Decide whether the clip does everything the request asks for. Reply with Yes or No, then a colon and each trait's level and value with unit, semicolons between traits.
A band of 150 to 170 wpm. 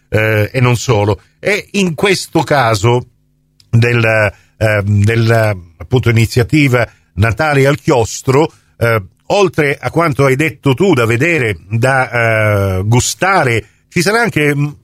No: average, 120 wpm